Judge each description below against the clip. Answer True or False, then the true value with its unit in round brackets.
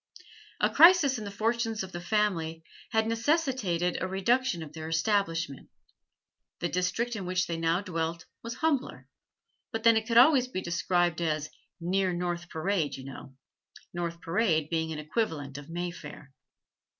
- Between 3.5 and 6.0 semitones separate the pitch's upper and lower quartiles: True (5.3 semitones)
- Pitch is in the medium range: True (180 Hz)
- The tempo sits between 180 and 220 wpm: False (155 wpm)